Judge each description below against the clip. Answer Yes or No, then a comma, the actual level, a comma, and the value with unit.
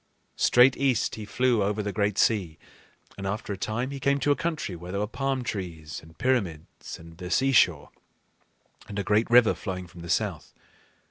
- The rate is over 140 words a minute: Yes, average, 175 wpm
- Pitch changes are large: Yes, wide, 5.7 semitones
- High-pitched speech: No, low, 105 Hz